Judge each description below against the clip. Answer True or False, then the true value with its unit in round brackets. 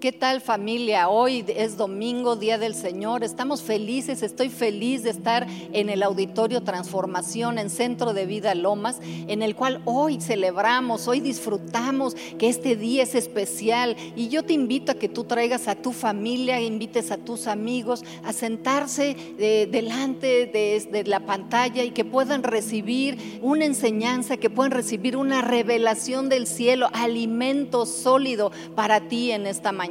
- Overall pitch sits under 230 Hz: False (235 Hz)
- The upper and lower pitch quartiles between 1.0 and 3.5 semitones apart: True (3.0 semitones)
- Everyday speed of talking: True (160 wpm)